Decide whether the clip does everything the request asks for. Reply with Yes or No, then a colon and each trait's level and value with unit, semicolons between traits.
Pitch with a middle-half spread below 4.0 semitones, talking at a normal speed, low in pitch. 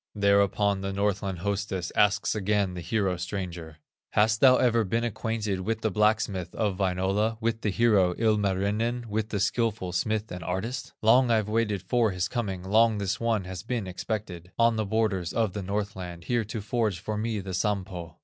Yes: average, 2.9 semitones; average, 180 wpm; low, 105 Hz